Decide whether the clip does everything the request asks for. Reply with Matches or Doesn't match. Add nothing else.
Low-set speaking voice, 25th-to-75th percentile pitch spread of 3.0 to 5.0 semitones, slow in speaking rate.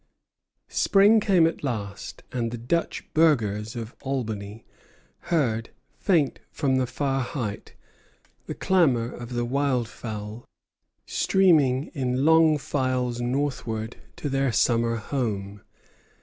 Matches